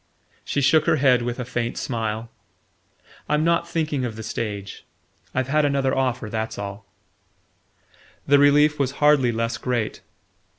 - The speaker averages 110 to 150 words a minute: Yes, average, 145 wpm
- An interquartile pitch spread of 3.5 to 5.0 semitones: Yes, average, 3.9 semitones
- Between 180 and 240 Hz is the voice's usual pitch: No, low, 130 Hz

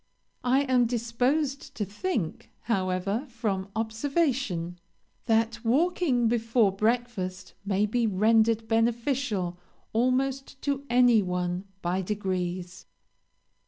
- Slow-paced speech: Yes, slow, 95 wpm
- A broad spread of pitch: No, average, 4.5 semitones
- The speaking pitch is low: No, high, 225 Hz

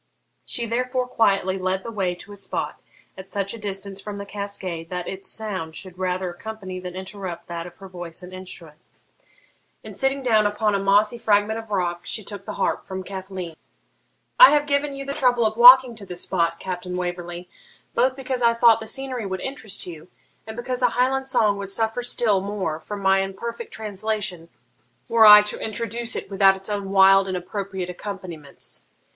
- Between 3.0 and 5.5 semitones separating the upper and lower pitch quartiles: Yes, average, 3.5 semitones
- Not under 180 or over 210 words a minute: Yes, average, 190 wpm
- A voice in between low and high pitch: No, high, 200 Hz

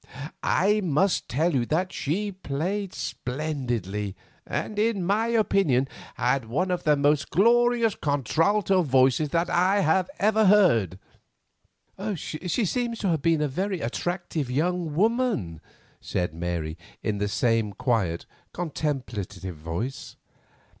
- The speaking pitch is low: No, medium, 155 Hz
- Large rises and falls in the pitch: Yes, wide, 8.0 semitones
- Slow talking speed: Yes, slow, 120 wpm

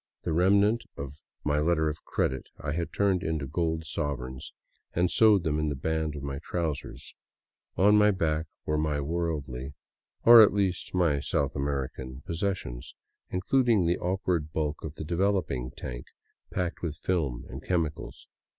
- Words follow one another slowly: No, average, 165 wpm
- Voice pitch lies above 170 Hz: No, very low, 80 Hz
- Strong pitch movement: No, average, 4.1 semitones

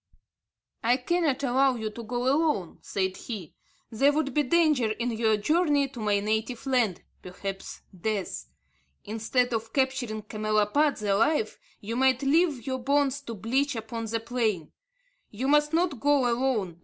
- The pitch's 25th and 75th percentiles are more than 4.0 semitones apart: Yes, average, 4.4 semitones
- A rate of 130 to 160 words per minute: Yes, average, 150 wpm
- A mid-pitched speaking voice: No, high, 245 Hz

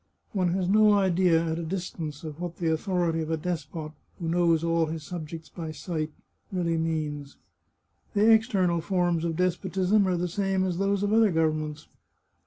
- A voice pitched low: No, medium, 170 Hz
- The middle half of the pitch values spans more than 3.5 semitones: No, average, 2.7 semitones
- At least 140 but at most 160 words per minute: No, average, 180 wpm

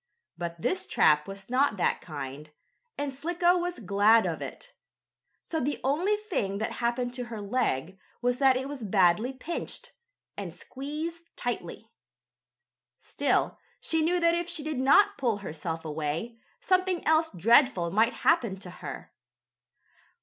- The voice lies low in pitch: No, very high, 250 Hz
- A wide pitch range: Yes, wide, 8.8 semitones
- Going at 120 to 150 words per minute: Yes, average, 145 wpm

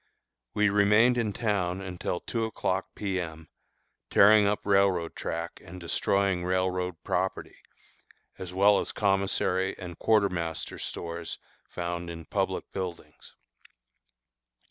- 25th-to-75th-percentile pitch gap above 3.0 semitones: No, narrow, 2.5 semitones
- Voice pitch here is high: No, very low, 95 Hz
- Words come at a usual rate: No, slow, 110 wpm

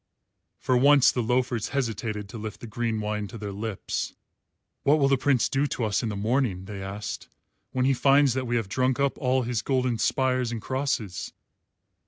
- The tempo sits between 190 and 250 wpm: Yes, average, 195 wpm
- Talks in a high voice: No, low, 120 Hz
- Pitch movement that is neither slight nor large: Yes, average, 3.5 semitones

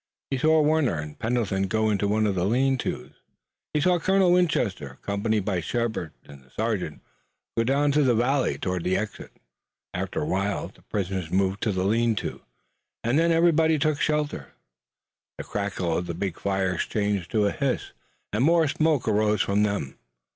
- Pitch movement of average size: No, wide, 6.7 semitones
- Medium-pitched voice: No, low, 110 Hz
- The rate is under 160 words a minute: No, average, 180 wpm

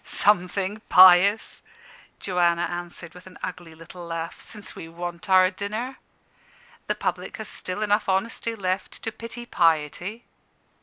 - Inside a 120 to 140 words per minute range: Yes, slow, 135 wpm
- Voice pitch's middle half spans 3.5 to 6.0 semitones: No, average, 3.1 semitones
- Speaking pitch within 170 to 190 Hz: Yes, medium, 185 Hz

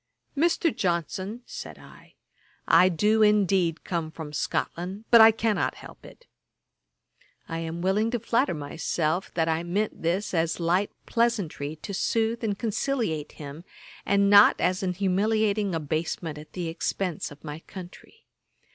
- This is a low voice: No, medium, 185 Hz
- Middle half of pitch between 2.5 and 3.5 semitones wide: No, average, 4.6 semitones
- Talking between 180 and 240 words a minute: No, average, 145 wpm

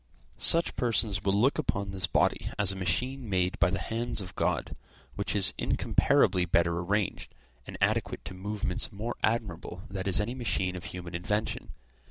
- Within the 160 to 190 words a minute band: Yes, average, 170 wpm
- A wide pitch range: No, average, 3.4 semitones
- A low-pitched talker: Yes, low, 100 Hz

